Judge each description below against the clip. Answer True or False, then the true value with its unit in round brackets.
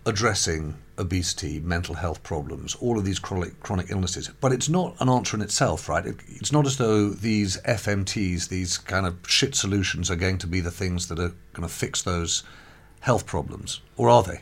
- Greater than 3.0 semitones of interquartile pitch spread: True (3.7 semitones)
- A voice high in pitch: False (95 Hz)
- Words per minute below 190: False (200 wpm)